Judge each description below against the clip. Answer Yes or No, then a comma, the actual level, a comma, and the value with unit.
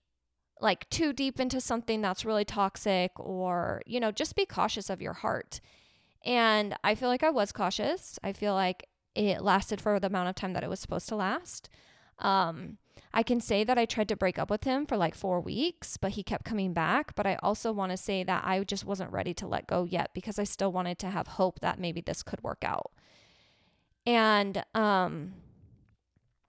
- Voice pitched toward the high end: Yes, high, 195 Hz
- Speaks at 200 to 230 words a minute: Yes, fast, 205 wpm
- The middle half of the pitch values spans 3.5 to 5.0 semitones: No, average, 3.1 semitones